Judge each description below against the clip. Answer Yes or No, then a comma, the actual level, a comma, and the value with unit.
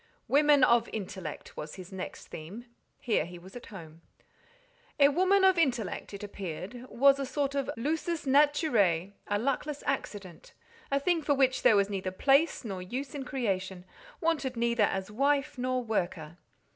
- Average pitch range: No, wide, 6.7 semitones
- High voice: Yes, high, 240 Hz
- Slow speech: No, average, 160 wpm